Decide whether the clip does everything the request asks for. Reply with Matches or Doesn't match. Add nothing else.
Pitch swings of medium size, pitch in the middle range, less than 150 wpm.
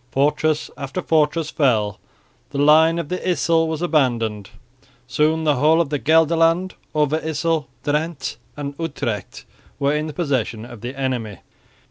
Matches